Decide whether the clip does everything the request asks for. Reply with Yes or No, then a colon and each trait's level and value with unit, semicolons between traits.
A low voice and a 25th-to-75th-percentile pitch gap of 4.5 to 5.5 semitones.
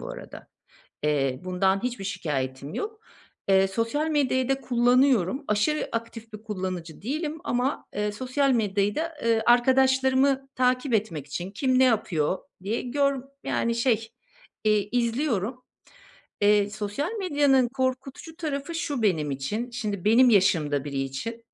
No: high, 230 Hz; average, 5.2 semitones